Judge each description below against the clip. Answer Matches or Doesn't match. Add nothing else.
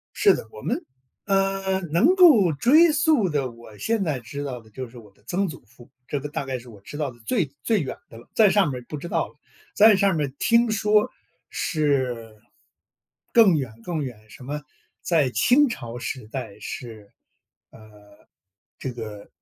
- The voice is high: Doesn't match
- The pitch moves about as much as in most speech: Doesn't match